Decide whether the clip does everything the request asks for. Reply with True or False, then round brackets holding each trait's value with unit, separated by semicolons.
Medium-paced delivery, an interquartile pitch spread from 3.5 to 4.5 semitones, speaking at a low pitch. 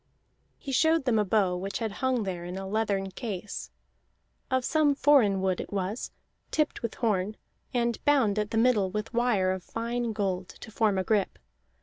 False (185 wpm; 4.0 semitones; 215 Hz)